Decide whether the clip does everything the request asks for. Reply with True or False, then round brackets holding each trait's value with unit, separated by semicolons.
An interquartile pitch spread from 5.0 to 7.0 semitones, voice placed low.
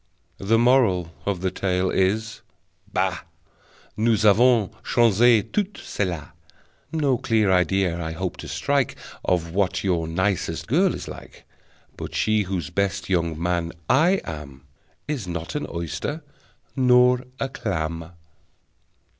True (5.5 semitones; 95 Hz)